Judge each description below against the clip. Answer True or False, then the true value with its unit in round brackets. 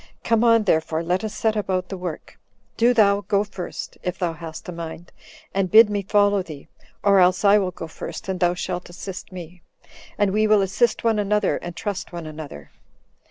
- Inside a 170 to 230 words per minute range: True (200 wpm)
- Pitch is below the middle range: False (190 Hz)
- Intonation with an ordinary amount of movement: True (3.0 semitones)